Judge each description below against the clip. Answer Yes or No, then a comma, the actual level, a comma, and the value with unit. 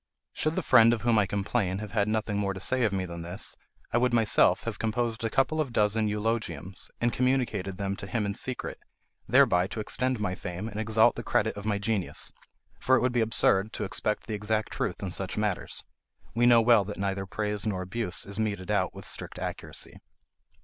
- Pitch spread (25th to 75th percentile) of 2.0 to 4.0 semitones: Yes, average, 2.9 semitones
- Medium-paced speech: No, fast, 215 wpm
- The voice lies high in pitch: No, low, 105 Hz